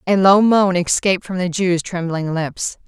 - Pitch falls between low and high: Yes, medium, 180 Hz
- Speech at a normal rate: Yes, average, 190 wpm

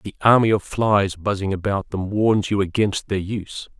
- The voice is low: Yes, low, 100 Hz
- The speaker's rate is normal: Yes, average, 190 wpm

